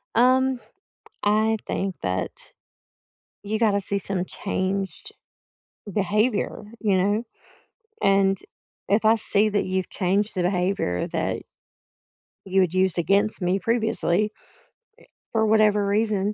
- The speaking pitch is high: Yes, high, 200 Hz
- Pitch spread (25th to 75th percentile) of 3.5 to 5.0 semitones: No, narrow, 2.4 semitones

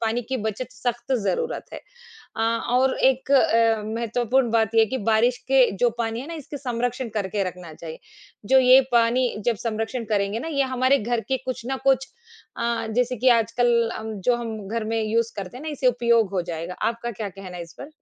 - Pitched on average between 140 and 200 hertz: No, high, 235 Hz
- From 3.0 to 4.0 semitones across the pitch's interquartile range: No, narrow, 2.6 semitones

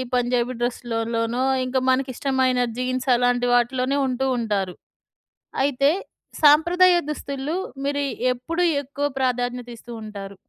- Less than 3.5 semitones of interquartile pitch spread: Yes, narrow, 2.4 semitones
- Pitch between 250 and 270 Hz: Yes, very high, 255 Hz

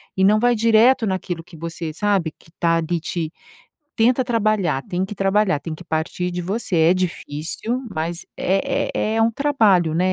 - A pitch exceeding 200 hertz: No, medium, 185 Hz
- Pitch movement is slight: No, average, 4.4 semitones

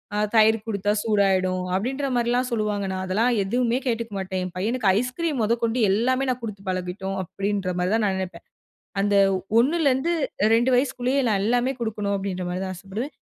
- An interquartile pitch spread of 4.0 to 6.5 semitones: Yes, average, 4.3 semitones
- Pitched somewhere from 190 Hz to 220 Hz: Yes, high, 215 Hz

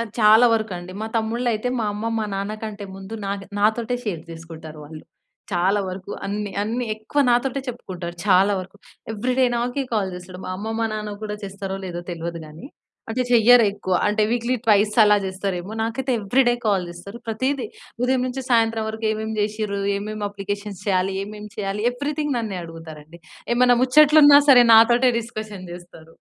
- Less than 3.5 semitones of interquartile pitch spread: No, average, 3.8 semitones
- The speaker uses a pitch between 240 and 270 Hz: No, high, 210 Hz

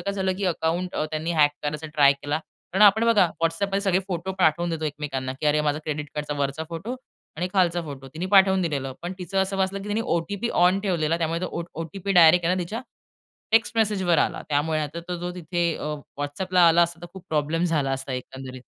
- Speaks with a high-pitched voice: No, medium, 170 Hz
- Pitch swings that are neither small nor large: Yes, average, 3.9 semitones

